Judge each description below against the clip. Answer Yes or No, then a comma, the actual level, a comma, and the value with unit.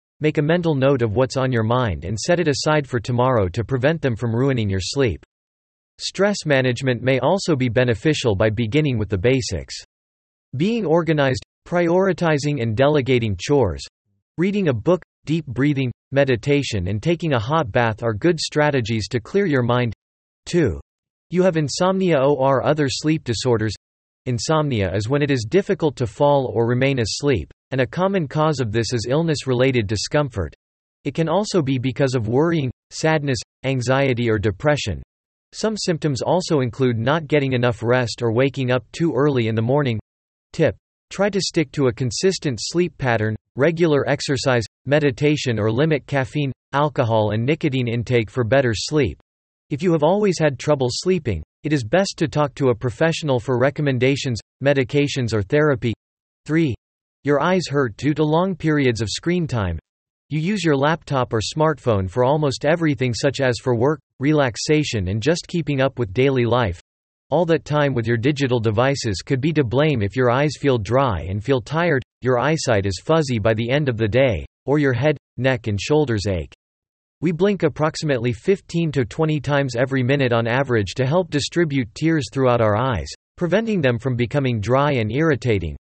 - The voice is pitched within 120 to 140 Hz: Yes, low, 135 Hz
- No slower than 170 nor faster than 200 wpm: Yes, average, 175 wpm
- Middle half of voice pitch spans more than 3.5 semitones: Yes, average, 4.5 semitones